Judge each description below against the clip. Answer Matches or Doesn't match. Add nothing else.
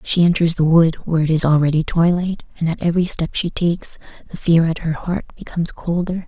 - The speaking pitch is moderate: Matches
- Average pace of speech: Doesn't match